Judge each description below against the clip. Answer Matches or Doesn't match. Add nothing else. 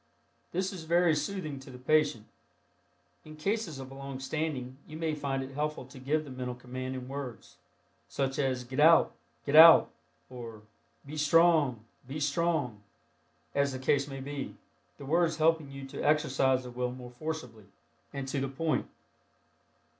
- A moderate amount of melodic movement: Matches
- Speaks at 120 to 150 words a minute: Doesn't match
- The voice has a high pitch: Doesn't match